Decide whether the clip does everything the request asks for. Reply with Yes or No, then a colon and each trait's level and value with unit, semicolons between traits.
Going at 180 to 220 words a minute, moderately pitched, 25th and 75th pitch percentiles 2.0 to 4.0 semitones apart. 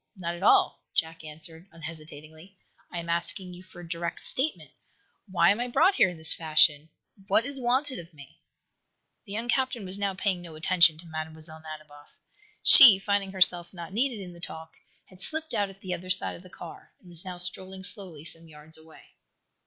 Yes: average, 195 wpm; medium, 175 Hz; average, 3.4 semitones